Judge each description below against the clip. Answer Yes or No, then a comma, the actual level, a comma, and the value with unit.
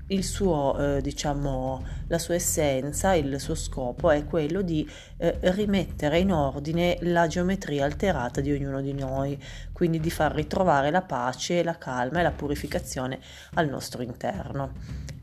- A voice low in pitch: No, medium, 150 Hz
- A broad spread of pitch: No, average, 3.9 semitones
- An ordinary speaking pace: Yes, average, 150 wpm